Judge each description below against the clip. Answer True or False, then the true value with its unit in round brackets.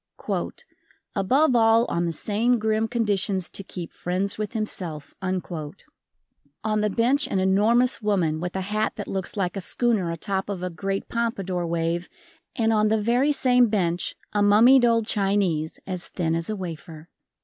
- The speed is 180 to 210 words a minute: False (160 wpm)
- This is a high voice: True (200 Hz)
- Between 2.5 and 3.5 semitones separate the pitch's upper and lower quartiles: False (4.0 semitones)